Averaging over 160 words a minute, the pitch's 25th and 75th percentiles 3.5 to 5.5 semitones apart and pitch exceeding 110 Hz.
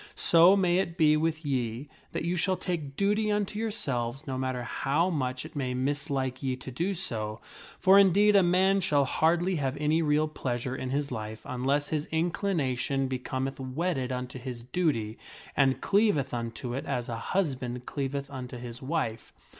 Yes: average, 180 wpm; average, 5.1 semitones; medium, 140 Hz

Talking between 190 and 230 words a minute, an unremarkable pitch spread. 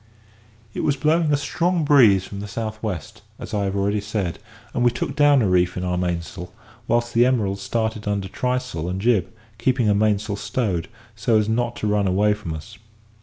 Yes: average, 200 wpm; average, 3.8 semitones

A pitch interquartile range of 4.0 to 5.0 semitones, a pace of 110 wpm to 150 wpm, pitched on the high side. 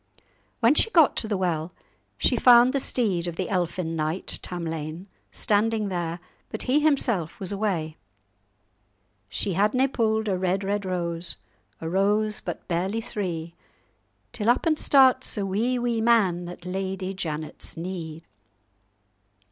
Yes: average, 4.6 semitones; average, 140 wpm; high, 195 Hz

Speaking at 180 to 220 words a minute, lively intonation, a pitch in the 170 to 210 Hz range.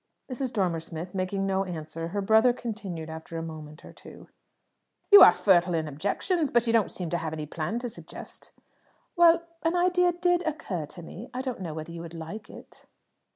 Yes: average, 200 wpm; wide, 7.1 semitones; high, 190 Hz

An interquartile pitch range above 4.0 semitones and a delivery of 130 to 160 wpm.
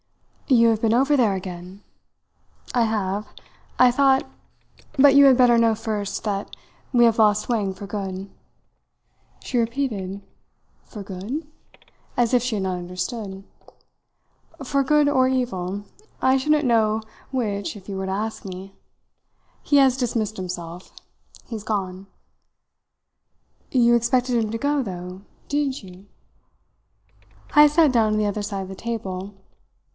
Yes: average, 4.6 semitones; average, 140 wpm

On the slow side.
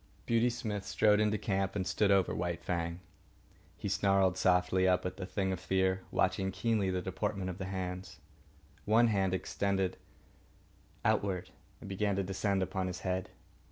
No: average, 160 wpm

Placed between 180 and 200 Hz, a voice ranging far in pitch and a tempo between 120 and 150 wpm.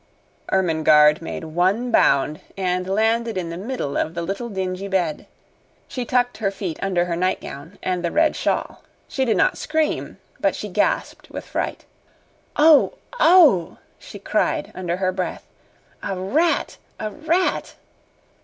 Yes: high, 190 Hz; wide, 5.8 semitones; average, 145 wpm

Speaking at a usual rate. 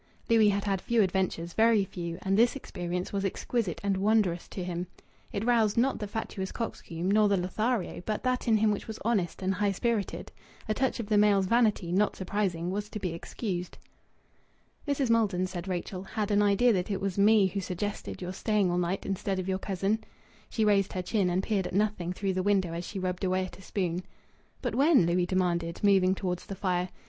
No: fast, 210 wpm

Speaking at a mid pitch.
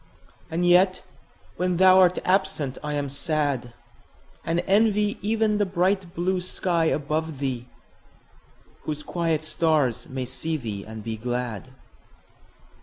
Yes: medium, 160 Hz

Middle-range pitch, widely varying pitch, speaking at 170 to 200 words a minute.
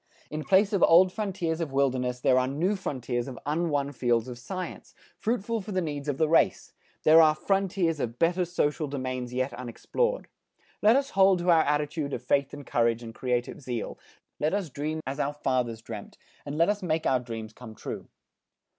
Yes: medium, 145 Hz; wide, 5.7 semitones; average, 190 wpm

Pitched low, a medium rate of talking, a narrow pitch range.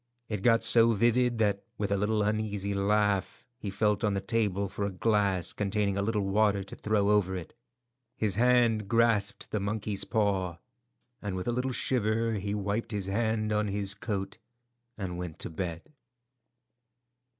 Yes: low, 105 Hz; average, 170 wpm; narrow, 1.9 semitones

